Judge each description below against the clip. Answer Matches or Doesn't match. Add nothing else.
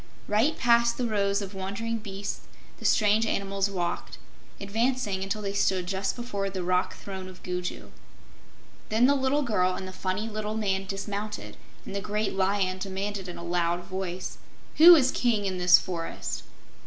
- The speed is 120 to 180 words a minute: Matches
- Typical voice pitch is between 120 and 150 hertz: Doesn't match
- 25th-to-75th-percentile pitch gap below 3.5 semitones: Matches